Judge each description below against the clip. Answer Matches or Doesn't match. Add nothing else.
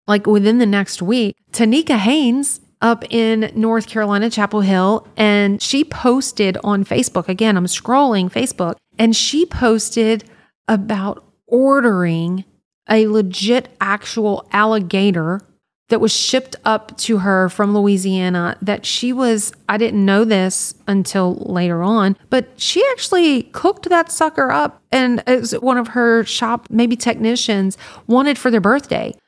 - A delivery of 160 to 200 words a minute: Doesn't match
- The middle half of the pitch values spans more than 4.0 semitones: Doesn't match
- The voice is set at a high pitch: Matches